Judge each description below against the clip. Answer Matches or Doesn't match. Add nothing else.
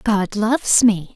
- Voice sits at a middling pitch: Doesn't match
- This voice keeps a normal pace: Matches